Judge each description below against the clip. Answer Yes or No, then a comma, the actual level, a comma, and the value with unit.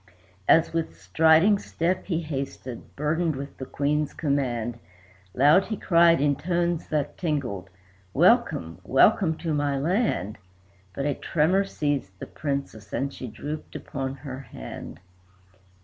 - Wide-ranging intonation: No, average, 3.8 semitones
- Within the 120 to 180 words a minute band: Yes, slow, 135 wpm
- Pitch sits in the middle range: Yes, medium, 145 Hz